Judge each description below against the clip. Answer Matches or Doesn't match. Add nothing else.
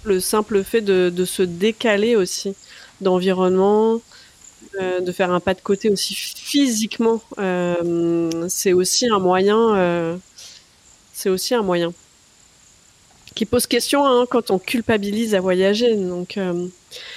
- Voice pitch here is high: Matches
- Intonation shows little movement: Doesn't match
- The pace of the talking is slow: Matches